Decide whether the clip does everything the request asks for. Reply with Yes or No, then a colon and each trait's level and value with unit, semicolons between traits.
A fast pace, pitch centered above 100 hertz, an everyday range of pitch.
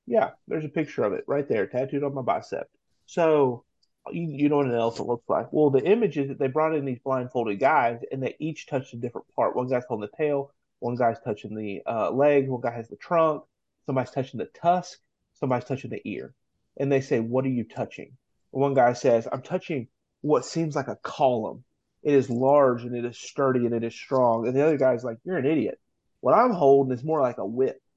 Yes: fast, 230 wpm; low, 135 Hz; average, 3.5 semitones